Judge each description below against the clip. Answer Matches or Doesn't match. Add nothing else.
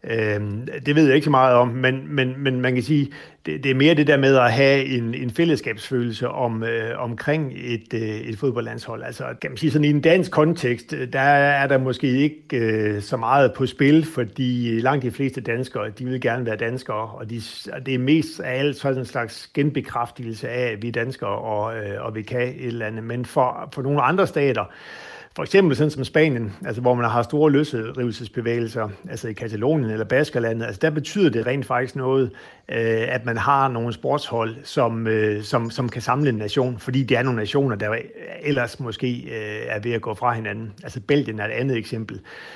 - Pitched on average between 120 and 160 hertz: Matches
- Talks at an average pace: Matches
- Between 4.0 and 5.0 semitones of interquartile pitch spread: Doesn't match